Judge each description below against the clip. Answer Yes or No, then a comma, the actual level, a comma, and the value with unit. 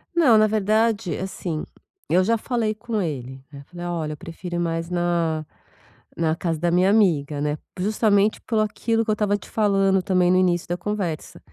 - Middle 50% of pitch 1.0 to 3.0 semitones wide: No, average, 4.4 semitones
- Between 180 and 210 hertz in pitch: Yes, medium, 185 Hz